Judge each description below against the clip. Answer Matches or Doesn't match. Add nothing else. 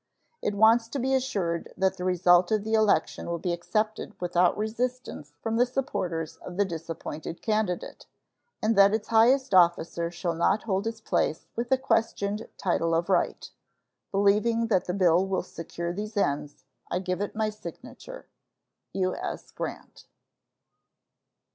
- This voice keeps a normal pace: Matches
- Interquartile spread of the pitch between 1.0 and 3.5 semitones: Doesn't match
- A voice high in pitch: Matches